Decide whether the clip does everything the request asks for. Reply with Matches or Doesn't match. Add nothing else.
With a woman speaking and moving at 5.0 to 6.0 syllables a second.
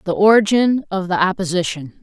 Matches